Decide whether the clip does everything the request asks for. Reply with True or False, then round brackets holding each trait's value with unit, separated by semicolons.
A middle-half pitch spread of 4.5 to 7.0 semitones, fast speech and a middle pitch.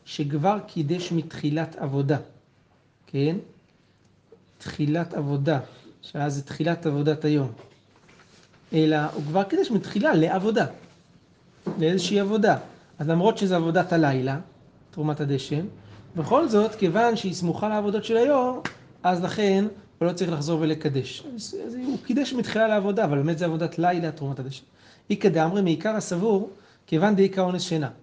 False (5.1 semitones; 135 wpm; 170 Hz)